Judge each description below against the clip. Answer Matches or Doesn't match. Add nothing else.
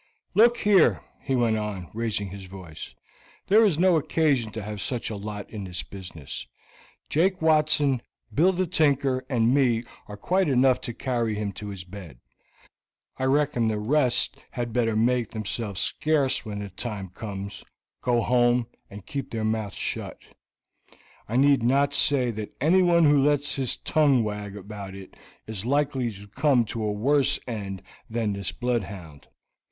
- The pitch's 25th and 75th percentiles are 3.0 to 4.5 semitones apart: Doesn't match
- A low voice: Matches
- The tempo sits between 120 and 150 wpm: Doesn't match